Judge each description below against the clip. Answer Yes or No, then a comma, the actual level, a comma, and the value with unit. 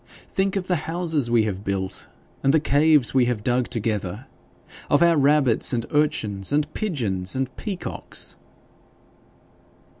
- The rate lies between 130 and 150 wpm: Yes, average, 140 wpm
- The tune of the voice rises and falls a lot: Yes, wide, 6.2 semitones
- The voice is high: No, low, 135 Hz